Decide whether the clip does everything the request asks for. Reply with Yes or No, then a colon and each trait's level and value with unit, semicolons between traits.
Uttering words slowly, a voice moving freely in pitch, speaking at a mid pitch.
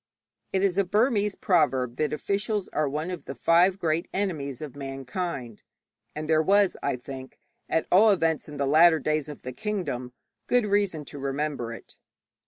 No: average, 175 wpm; wide, 5.8 semitones; medium, 155 Hz